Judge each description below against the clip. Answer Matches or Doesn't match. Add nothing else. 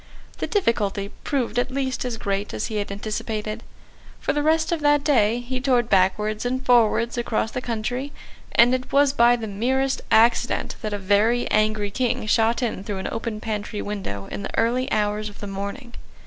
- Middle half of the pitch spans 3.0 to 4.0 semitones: Matches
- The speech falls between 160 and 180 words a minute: Doesn't match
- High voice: Matches